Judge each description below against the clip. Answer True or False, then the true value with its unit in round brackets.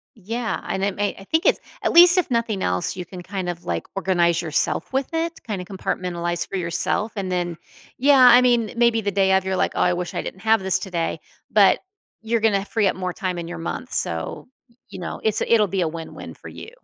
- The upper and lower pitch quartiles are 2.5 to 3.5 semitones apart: False (4.3 semitones)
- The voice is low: False (190 Hz)